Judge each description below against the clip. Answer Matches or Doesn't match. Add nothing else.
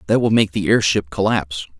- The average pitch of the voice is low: Matches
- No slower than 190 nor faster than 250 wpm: Matches